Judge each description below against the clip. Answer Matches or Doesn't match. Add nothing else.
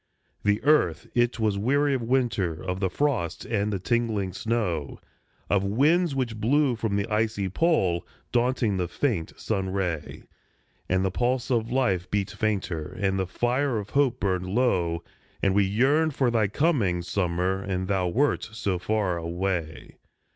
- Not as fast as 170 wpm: Matches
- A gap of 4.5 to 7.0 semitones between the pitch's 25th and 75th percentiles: Matches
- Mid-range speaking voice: Doesn't match